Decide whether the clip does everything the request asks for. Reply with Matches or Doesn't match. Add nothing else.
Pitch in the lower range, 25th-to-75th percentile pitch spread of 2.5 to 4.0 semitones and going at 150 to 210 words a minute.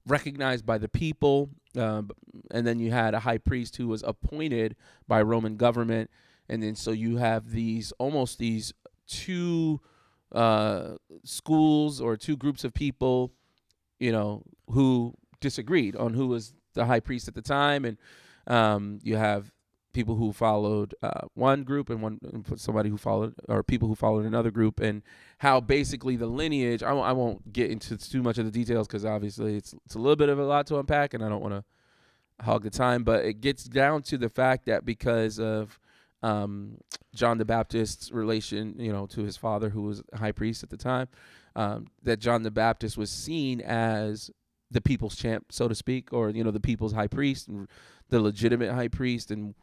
Matches